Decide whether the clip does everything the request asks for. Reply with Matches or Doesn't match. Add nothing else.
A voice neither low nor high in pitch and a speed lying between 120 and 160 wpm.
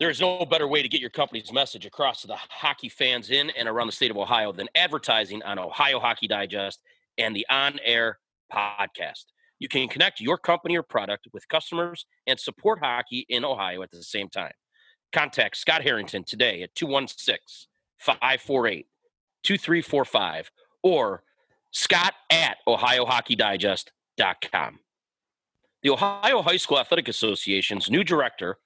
Matches